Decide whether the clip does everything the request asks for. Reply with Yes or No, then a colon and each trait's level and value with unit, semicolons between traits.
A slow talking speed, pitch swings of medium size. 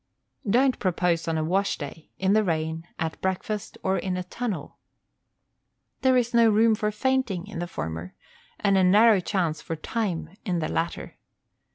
No: average, 170 wpm; average, 4.7 semitones